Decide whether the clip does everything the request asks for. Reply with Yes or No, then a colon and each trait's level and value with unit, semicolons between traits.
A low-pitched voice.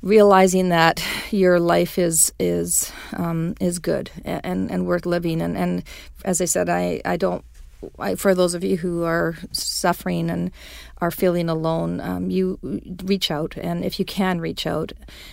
No: medium, 170 Hz